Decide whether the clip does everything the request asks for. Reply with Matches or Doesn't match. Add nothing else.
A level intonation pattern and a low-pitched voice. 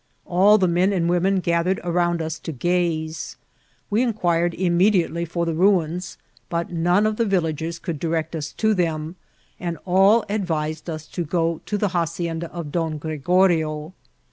Doesn't match